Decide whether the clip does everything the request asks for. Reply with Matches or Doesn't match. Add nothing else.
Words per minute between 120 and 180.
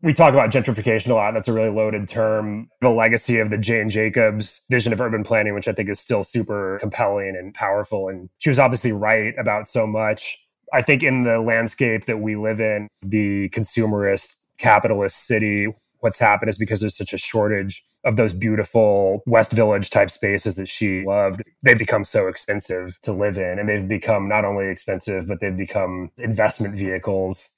Doesn't match